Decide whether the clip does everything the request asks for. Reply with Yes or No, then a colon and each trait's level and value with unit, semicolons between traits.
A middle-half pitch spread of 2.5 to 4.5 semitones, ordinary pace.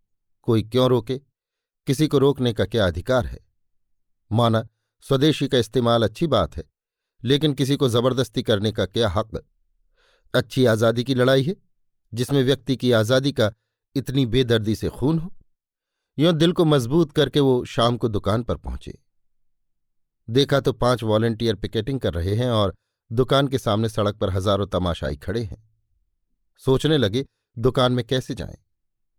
Yes: average, 3.9 semitones; average, 155 wpm